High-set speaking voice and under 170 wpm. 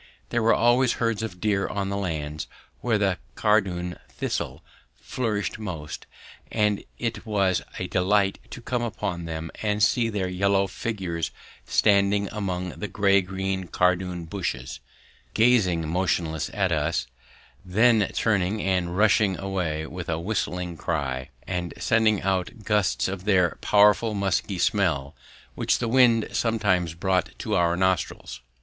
No: very low, 95 Hz; average, 140 wpm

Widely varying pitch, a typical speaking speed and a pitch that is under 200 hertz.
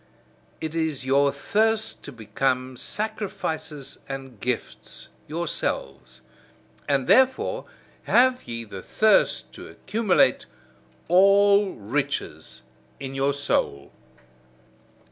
No: wide, 7.9 semitones; slow, 90 wpm; medium, 140 Hz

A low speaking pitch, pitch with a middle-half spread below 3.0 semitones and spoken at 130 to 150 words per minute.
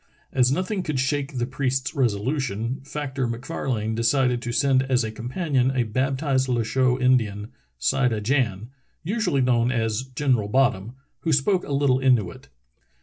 Yes: low, 130 Hz; narrow, 2.6 semitones; average, 145 wpm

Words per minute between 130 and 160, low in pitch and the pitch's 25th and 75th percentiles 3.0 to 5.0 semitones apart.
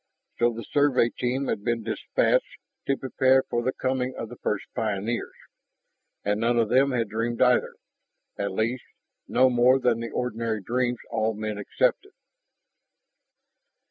No: average, 145 wpm; low, 120 Hz; narrow, 2.5 semitones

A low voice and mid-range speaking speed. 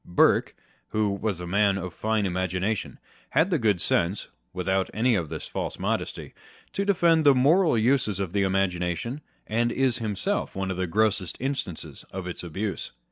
Yes: low, 100 Hz; average, 170 wpm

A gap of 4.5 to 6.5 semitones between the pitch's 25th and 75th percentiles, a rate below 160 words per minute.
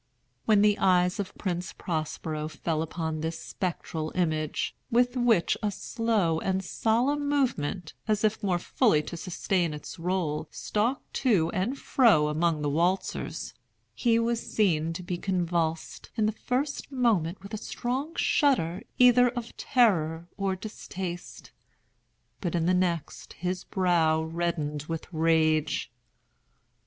Yes: average, 5.3 semitones; slow, 135 wpm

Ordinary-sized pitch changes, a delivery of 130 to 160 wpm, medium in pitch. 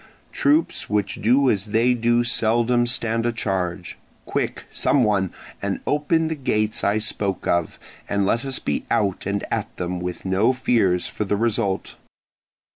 No: average, 3.7 semitones; average, 155 wpm; low, 110 Hz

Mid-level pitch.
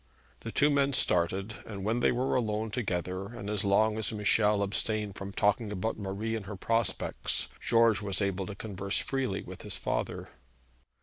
No: low, 105 Hz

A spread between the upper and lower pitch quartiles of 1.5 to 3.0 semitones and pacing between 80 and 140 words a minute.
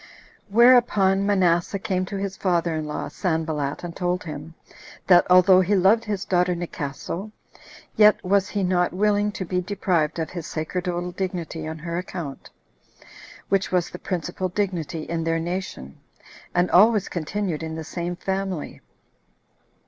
No: average, 2.7 semitones; average, 150 wpm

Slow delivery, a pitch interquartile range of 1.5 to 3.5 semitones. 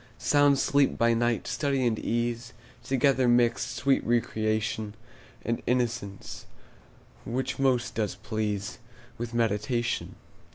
Yes: slow, 110 wpm; narrow, 2.6 semitones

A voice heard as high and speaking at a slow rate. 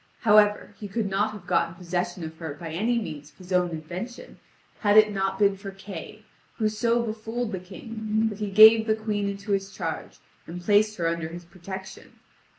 No: high, 200 Hz; average, 195 wpm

